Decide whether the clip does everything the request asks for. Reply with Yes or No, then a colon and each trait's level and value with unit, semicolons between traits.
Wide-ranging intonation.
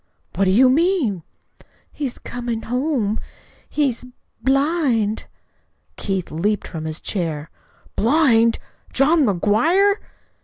Yes: wide, 6.3 semitones